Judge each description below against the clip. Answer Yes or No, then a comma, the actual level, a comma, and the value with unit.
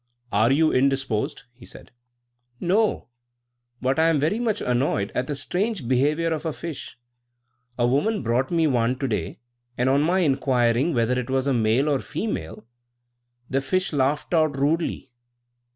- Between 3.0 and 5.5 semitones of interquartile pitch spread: Yes, average, 4.5 semitones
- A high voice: No, low, 135 Hz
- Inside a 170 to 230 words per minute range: No, average, 160 wpm